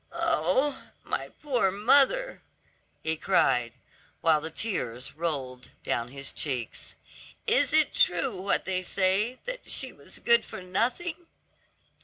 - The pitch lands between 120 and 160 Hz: No, medium, 185 Hz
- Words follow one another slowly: Yes, slow, 125 wpm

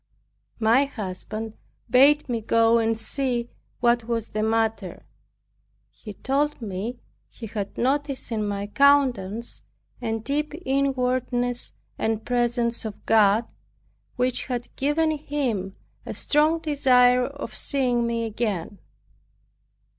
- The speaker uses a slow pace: Yes, slow, 115 wpm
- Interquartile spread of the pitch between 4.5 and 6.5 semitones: No, average, 3.4 semitones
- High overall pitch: Yes, high, 240 Hz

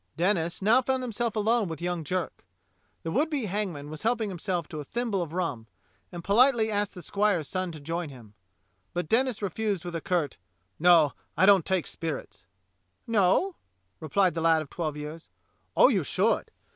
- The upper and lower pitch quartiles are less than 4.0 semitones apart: No, average, 4.7 semitones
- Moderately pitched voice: Yes, medium, 180 Hz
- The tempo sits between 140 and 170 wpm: No, average, 180 wpm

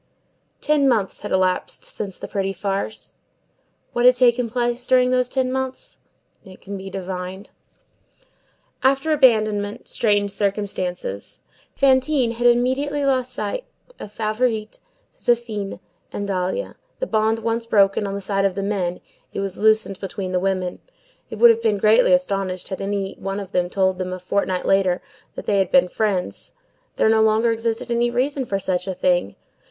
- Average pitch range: Yes, average, 3.9 semitones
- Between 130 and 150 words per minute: No, average, 160 wpm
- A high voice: Yes, high, 210 Hz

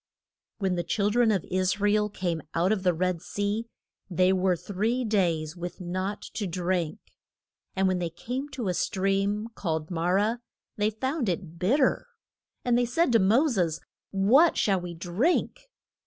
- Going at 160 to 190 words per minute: Yes, average, 170 wpm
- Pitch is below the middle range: No, high, 195 Hz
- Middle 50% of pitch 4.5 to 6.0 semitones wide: No, average, 3.7 semitones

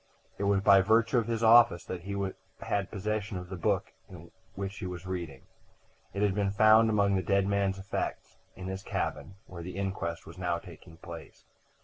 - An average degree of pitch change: No, narrow, 2.2 semitones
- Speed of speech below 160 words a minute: No, average, 195 wpm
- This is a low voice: Yes, very low, 95 Hz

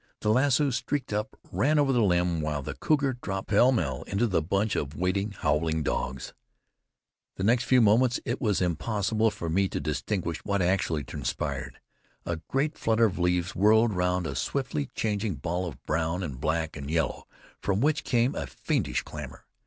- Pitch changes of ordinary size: No, wide, 6.0 semitones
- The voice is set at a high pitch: No, low, 100 Hz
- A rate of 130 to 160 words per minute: No, average, 175 wpm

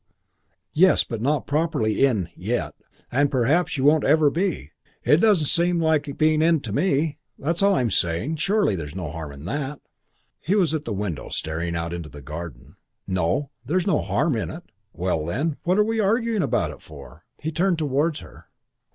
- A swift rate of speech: No, average, 185 wpm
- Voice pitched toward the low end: No, medium, 145 Hz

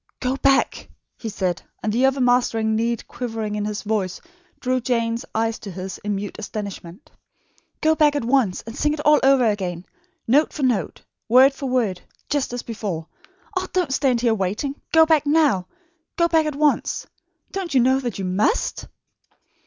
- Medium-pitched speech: No, high, 240 Hz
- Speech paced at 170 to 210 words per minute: Yes, average, 175 wpm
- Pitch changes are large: No, average, 4.7 semitones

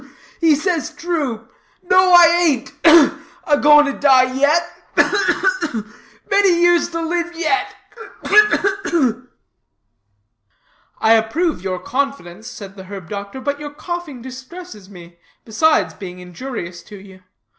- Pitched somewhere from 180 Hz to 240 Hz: No, very high, 280 Hz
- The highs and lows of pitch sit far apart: Yes, wide, 8.1 semitones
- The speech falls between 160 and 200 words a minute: No, average, 150 wpm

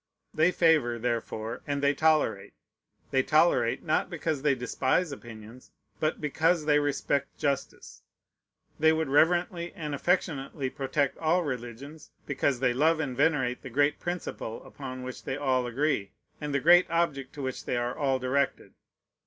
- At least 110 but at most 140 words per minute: No, average, 155 wpm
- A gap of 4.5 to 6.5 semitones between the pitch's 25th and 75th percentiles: No, average, 3.7 semitones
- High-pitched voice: No, medium, 140 Hz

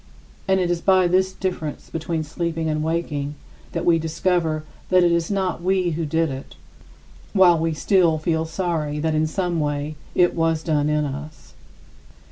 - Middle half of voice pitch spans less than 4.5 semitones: Yes, narrow, 2.4 semitones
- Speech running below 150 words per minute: No, average, 170 wpm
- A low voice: No, medium, 165 Hz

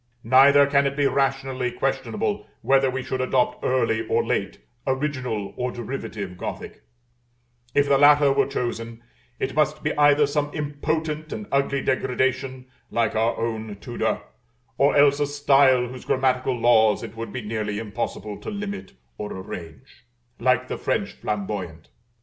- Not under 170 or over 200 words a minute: No, average, 150 wpm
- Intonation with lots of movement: No, average, 3.7 semitones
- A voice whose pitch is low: Yes, low, 130 Hz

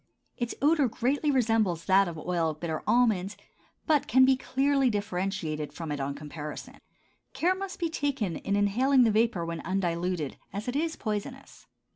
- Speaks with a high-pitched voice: Yes, high, 205 Hz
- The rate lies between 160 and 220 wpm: Yes, average, 165 wpm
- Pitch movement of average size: No, wide, 7.5 semitones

